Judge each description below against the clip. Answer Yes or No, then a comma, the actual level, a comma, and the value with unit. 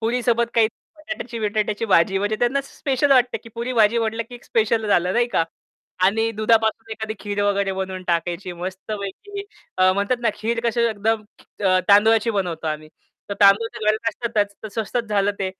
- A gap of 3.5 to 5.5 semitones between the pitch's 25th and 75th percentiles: No, average, 2.7 semitones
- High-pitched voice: Yes, high, 215 Hz